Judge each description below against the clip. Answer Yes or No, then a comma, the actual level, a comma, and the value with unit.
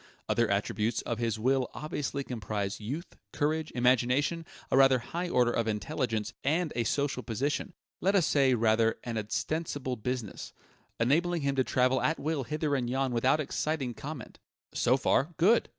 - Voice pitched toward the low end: Yes, low, 130 Hz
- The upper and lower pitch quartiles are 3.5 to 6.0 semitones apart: Yes, average, 4.4 semitones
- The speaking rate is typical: Yes, average, 160 wpm